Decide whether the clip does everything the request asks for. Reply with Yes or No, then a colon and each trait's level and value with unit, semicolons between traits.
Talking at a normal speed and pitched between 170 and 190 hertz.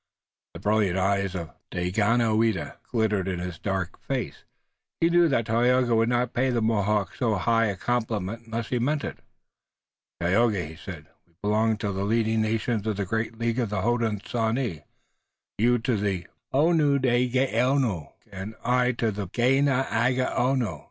No: average, 150 wpm; low, 115 Hz